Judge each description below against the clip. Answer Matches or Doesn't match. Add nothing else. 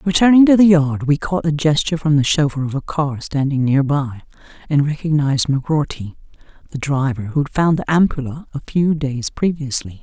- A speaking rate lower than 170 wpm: Doesn't match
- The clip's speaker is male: Doesn't match